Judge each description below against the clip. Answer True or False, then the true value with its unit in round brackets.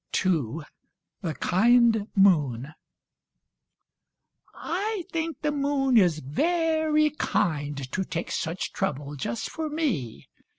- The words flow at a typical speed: False (100 wpm)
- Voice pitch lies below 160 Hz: False (200 Hz)